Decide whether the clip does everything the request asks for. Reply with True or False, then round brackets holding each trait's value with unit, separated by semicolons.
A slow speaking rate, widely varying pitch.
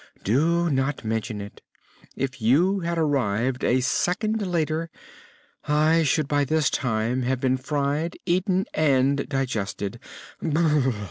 False (120 wpm; 4.4 semitones)